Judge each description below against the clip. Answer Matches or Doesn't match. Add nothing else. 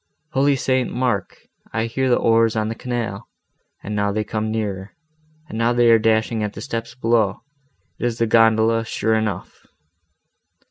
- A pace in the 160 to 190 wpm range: Matches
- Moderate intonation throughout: Doesn't match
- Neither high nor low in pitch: Doesn't match